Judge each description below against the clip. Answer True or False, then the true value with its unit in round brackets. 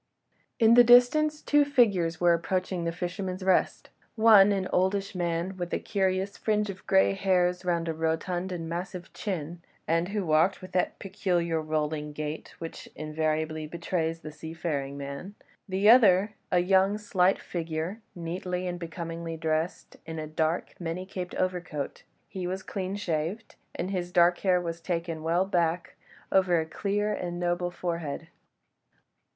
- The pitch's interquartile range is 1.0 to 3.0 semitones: True (2.6 semitones)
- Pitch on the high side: False (175 Hz)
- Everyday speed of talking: True (155 wpm)